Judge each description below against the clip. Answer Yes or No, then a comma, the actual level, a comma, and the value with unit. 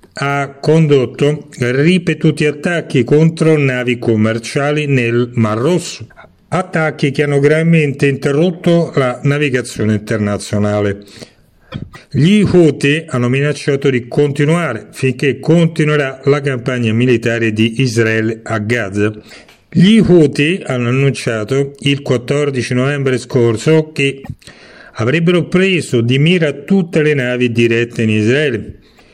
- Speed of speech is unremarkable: No, slow, 105 wpm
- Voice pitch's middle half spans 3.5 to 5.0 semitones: Yes, average, 4.4 semitones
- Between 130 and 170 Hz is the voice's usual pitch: Yes, medium, 140 Hz